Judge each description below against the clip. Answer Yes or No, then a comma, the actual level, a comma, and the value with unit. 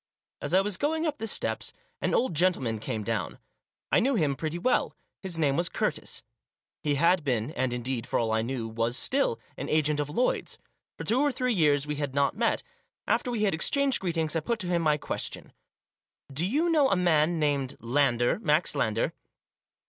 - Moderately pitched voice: Yes, medium, 155 Hz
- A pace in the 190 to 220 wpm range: Yes, average, 195 wpm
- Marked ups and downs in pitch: Yes, wide, 7.2 semitones